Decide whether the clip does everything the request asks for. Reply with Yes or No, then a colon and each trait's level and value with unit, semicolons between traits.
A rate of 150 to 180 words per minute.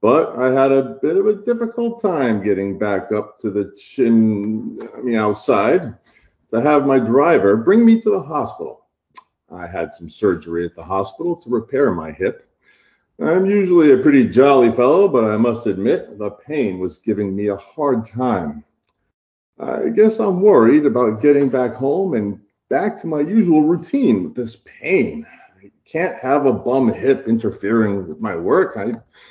Yes: average, 170 wpm